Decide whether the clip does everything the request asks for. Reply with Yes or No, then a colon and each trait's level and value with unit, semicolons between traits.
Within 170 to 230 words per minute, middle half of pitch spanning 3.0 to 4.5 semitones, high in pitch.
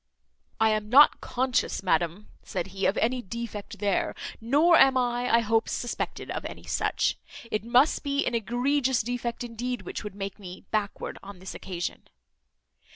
No: average, 160 wpm; average, 3.6 semitones; high, 230 Hz